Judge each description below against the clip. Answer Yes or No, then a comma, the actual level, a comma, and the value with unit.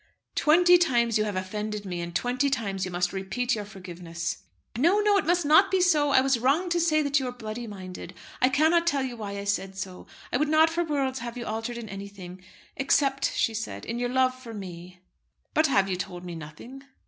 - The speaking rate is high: Yes, fast, 220 wpm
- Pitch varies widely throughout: Yes, wide, 6.8 semitones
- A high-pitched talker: Yes, high, 235 Hz